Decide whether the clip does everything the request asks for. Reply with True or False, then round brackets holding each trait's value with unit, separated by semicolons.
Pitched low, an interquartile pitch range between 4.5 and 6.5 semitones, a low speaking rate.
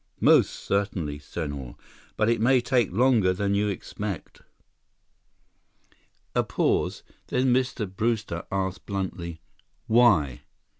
True (100 Hz; 5.2 semitones; 100 wpm)